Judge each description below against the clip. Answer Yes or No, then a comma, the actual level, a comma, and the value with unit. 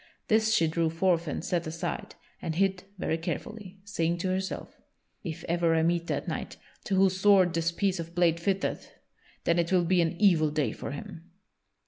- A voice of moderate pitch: Yes, medium, 170 Hz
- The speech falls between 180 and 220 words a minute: Yes, average, 185 wpm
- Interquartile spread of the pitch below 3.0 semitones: Yes, narrow, 2.4 semitones